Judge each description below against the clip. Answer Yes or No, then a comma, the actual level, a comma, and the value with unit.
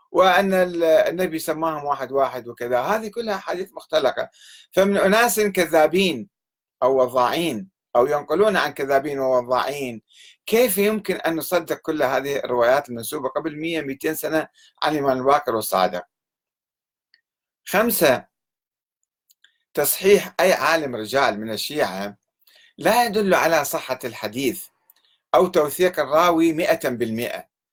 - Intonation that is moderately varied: No, wide, 5.9 semitones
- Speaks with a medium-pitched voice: Yes, medium, 160 Hz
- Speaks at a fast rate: No, average, 115 wpm